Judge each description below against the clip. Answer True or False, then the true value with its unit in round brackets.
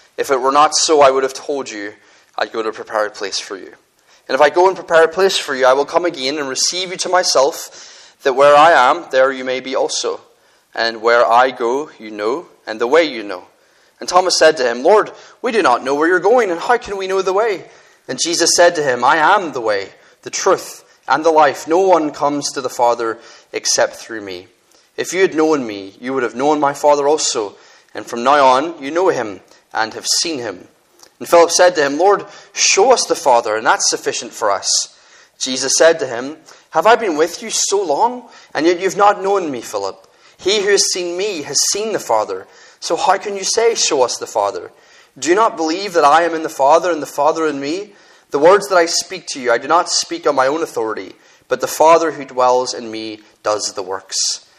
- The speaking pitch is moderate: True (170 Hz)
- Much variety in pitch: True (8.7 semitones)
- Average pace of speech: False (235 wpm)